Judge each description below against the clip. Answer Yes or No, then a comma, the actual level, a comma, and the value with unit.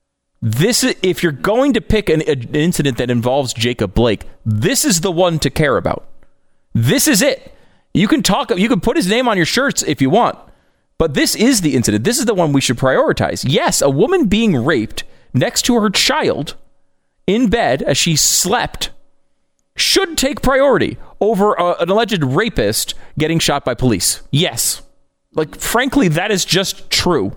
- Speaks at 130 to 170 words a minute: No, average, 180 wpm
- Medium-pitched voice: Yes, medium, 170 Hz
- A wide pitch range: Yes, wide, 8.6 semitones